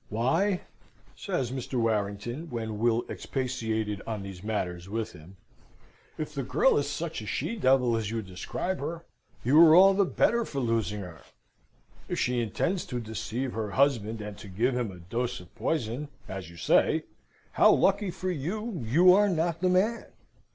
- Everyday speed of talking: Yes, average, 170 wpm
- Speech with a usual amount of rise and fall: No, wide, 7.6 semitones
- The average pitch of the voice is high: No, low, 120 Hz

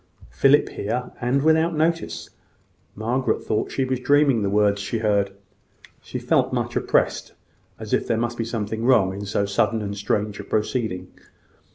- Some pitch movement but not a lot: Yes, average, 4.1 semitones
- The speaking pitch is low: Yes, low, 110 Hz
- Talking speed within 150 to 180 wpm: Yes, average, 165 wpm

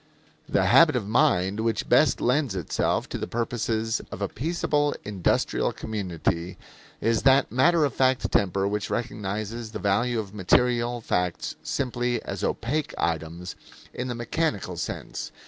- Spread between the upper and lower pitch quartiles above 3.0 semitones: Yes, average, 4.2 semitones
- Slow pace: No, average, 145 wpm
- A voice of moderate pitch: No, low, 115 Hz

